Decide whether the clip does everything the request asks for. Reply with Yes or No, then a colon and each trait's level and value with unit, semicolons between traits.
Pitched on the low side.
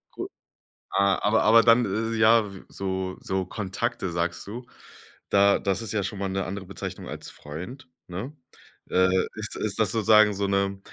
Yes: low, 100 Hz